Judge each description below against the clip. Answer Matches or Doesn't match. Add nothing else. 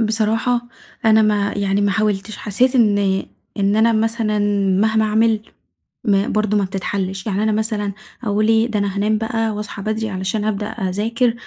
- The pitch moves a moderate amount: Doesn't match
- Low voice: Doesn't match